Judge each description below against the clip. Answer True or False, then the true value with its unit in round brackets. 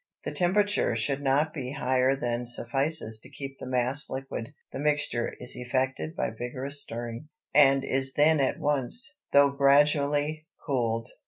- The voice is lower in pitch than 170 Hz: True (135 Hz)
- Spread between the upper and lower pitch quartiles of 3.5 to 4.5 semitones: False (3.1 semitones)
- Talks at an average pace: True (150 wpm)